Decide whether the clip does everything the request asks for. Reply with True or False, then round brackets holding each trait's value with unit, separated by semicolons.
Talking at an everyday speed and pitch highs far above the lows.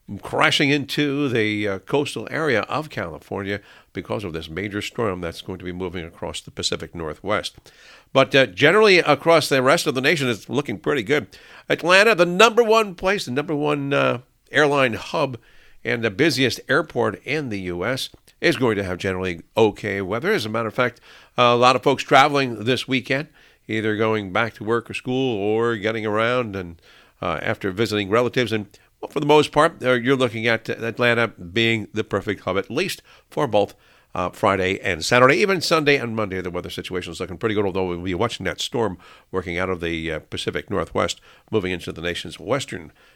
True (185 wpm; 5.9 semitones)